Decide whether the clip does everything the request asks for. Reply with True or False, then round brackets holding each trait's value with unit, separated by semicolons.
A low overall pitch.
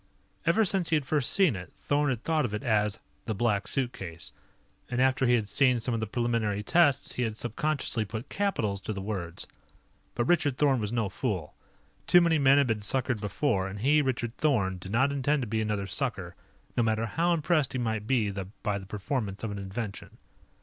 True (120 Hz)